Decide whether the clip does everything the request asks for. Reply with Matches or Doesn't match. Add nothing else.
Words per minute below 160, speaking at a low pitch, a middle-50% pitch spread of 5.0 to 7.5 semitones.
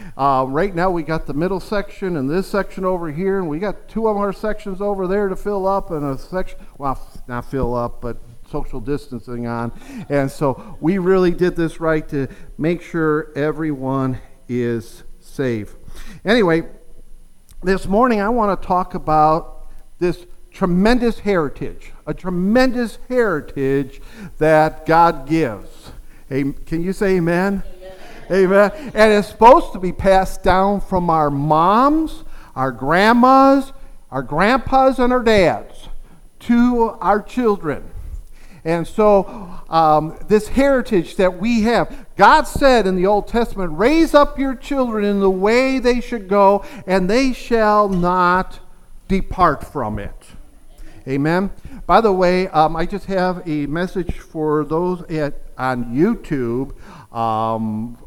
Doesn't match